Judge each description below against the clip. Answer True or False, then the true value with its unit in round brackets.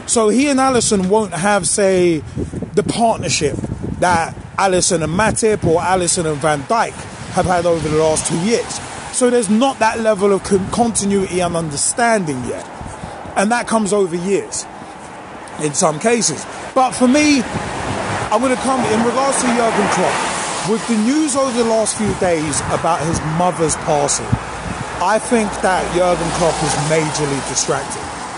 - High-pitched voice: True (195 Hz)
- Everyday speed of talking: True (160 wpm)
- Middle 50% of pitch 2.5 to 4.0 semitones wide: False (5.5 semitones)